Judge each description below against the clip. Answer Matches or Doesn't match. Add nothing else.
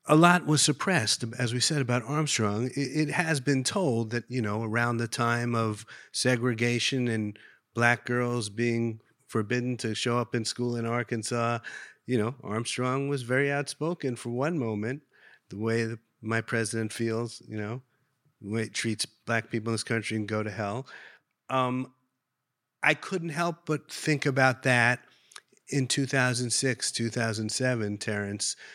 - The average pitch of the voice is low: Matches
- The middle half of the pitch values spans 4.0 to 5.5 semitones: Doesn't match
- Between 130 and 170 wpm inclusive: Matches